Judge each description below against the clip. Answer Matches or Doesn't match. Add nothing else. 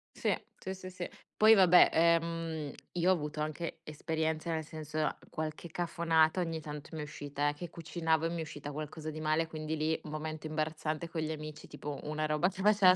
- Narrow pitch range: Matches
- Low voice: Doesn't match